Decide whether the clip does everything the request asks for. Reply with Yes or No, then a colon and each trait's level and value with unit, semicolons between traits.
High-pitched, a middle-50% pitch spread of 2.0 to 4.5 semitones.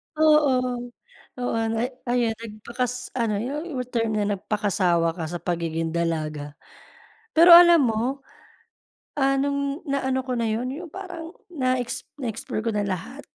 No: high, 240 Hz; average, 5.2 semitones